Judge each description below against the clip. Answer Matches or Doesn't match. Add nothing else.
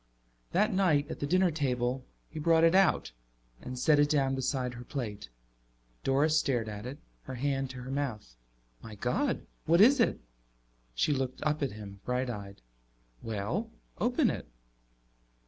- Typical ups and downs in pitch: Matches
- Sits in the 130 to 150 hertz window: Matches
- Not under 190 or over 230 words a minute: Doesn't match